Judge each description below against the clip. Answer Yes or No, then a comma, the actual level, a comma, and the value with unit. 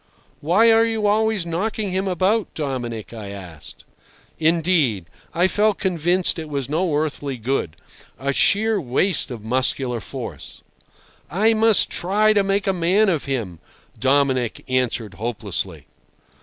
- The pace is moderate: No, slow, 130 wpm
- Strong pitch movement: Yes, wide, 7.6 semitones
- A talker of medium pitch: Yes, medium, 165 Hz